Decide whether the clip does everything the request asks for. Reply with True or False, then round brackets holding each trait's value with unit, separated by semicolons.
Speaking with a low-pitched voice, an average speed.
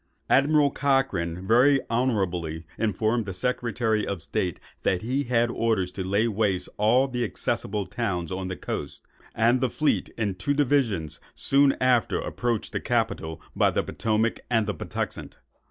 True (115 Hz; 155 wpm)